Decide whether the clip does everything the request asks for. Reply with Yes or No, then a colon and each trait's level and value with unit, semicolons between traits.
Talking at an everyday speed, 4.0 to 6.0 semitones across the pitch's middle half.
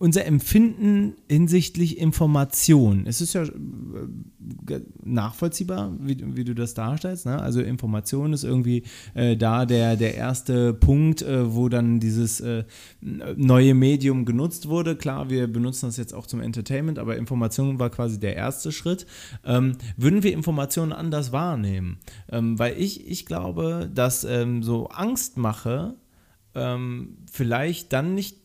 Yes: average, 145 wpm; wide, 5.4 semitones